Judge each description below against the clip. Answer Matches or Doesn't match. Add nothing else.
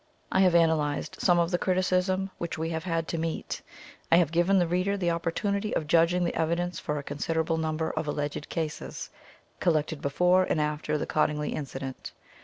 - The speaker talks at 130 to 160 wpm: Doesn't match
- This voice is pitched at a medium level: Matches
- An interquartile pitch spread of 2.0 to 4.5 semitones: Matches